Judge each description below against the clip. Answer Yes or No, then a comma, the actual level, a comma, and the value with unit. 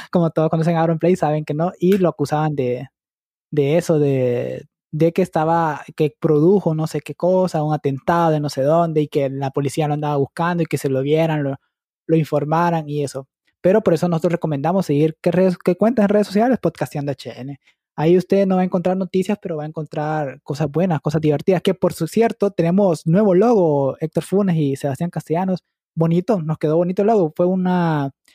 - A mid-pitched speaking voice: Yes, medium, 165 Hz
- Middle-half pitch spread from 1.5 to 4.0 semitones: Yes, average, 3.2 semitones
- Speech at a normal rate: No, fast, 205 wpm